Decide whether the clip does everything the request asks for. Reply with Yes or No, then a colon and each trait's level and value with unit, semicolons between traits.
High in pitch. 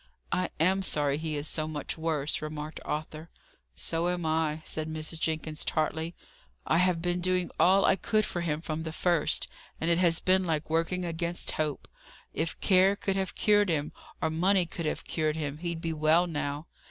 No: medium, 165 Hz